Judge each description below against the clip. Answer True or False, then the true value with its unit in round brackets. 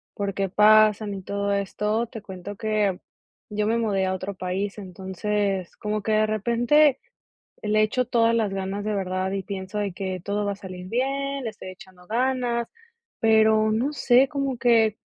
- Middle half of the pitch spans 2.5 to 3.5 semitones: True (2.8 semitones)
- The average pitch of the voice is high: True (210 Hz)